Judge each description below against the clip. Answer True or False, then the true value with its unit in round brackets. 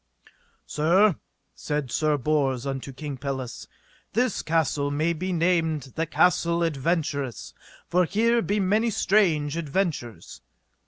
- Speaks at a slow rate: True (115 wpm)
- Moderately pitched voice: True (160 Hz)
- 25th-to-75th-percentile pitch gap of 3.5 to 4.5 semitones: True (4.1 semitones)